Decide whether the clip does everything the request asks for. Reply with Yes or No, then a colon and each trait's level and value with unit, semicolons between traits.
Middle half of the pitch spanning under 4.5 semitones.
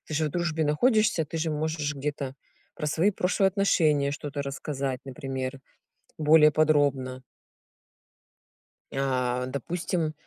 Yes: average, 2.7 semitones